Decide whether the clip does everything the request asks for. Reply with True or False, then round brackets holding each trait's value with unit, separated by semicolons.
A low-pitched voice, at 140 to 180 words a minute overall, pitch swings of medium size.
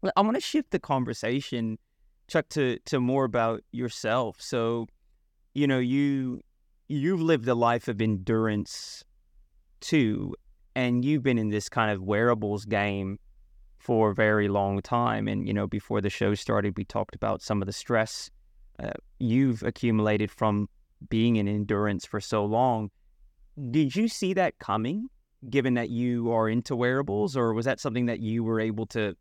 True (115 Hz; 165 wpm; 3.5 semitones)